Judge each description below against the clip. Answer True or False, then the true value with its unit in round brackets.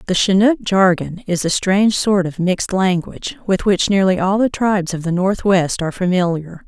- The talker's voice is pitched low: False (185 Hz)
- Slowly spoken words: False (190 wpm)